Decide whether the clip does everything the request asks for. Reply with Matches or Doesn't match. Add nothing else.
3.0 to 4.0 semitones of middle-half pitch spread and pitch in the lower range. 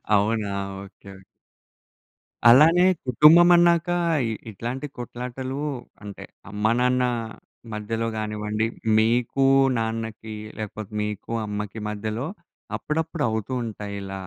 Matches